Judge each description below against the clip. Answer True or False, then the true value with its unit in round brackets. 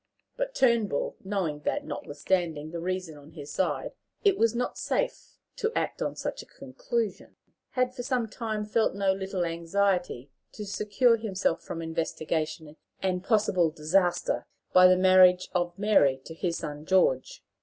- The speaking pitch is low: False (185 Hz)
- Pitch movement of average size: True (4.6 semitones)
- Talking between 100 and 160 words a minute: True (155 wpm)